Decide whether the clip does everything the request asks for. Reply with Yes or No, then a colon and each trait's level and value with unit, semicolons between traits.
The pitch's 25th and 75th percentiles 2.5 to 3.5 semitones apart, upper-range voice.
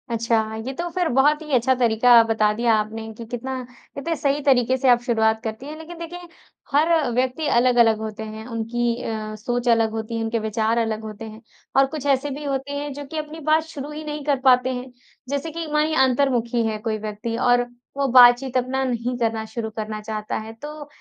No: average, 4.1 semitones; high, 245 Hz